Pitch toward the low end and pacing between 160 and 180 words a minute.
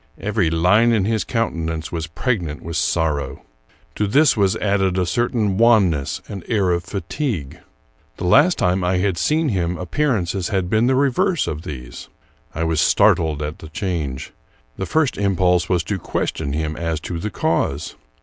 Yes: very low, 90 Hz; average, 170 wpm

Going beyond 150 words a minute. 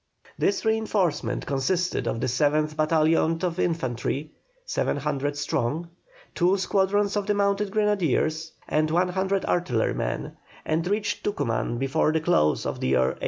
No: slow, 135 wpm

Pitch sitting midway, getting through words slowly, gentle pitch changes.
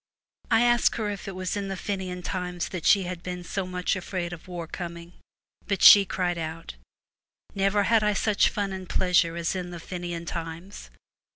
No: medium, 180 Hz; average, 195 wpm; narrow, 2.2 semitones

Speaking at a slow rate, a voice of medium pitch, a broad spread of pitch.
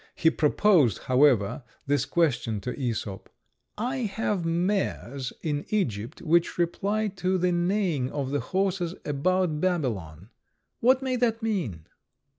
Yes: slow, 125 wpm; medium, 170 Hz; wide, 6.9 semitones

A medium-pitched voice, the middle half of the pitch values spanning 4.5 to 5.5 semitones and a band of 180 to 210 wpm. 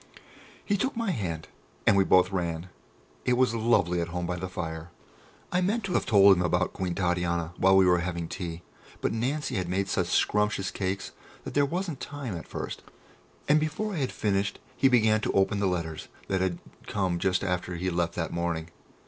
No: very low, 95 Hz; average, 5.2 semitones; average, 200 wpm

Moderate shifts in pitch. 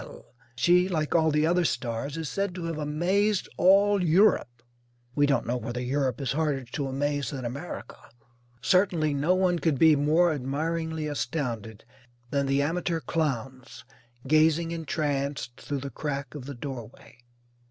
Yes: average, 3.7 semitones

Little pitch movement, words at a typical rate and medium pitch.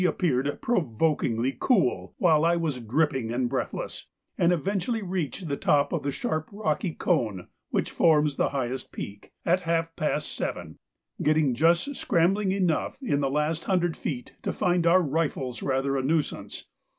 No: average, 4.5 semitones; average, 155 wpm; medium, 155 Hz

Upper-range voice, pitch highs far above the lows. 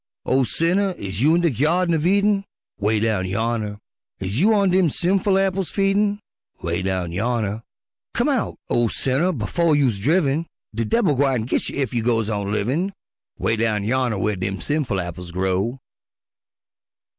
No: low, 125 Hz; wide, 8.8 semitones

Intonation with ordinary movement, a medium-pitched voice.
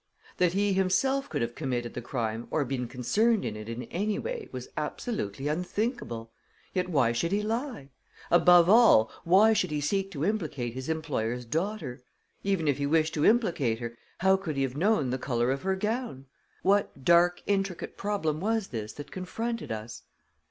No: wide, 8.1 semitones; medium, 165 Hz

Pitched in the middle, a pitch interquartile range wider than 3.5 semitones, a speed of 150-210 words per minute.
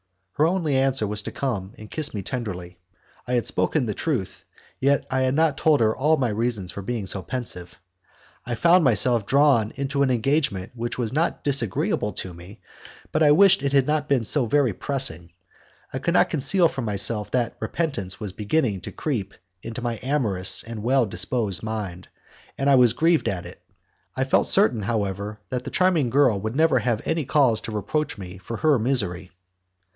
No: low, 120 Hz; average, 5.3 semitones; average, 190 wpm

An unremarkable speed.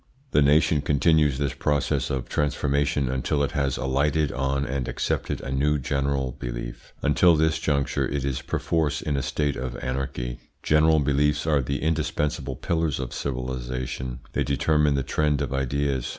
Yes: average, 160 wpm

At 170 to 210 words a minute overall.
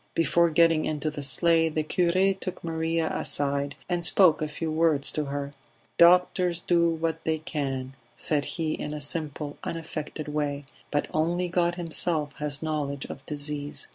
No: average, 160 wpm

